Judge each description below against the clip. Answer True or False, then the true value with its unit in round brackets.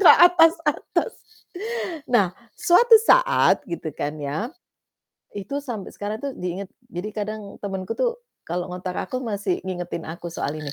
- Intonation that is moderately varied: False (8.1 semitones)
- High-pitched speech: True (205 Hz)